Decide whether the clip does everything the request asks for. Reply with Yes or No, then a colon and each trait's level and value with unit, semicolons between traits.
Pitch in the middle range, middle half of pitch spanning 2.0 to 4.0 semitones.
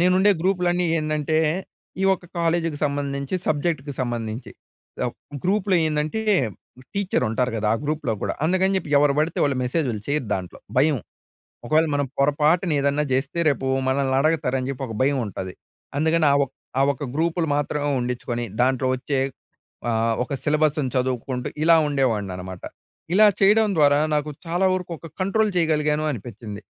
No: medium, 145 Hz; average, 4.4 semitones